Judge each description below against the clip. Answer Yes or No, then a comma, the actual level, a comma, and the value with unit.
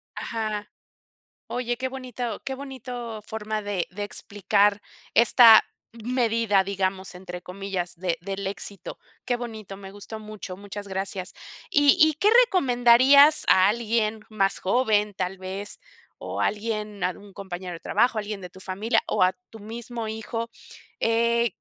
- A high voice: Yes, high, 215 Hz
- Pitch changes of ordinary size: Yes, average, 3.3 semitones